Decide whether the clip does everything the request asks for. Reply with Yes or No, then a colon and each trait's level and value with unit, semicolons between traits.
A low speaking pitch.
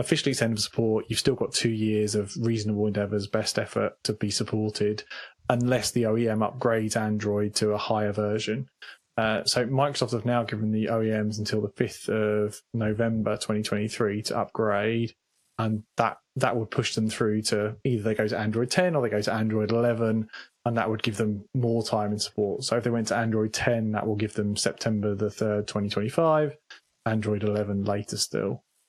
Yes: low, 110 Hz